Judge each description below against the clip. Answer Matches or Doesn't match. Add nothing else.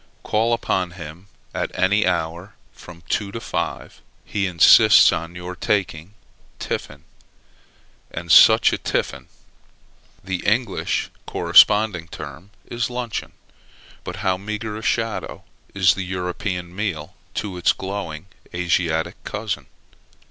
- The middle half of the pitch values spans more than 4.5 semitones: Doesn't match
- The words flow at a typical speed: Doesn't match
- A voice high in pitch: Doesn't match